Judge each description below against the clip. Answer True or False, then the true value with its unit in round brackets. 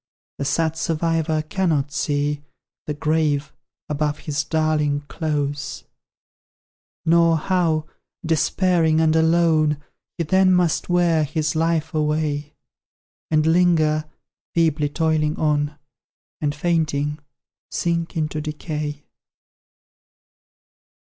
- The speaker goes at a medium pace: False (95 wpm)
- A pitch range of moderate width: False (1.6 semitones)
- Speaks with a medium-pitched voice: True (155 Hz)